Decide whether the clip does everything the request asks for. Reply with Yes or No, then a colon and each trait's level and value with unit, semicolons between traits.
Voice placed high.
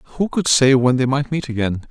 No: low, 135 Hz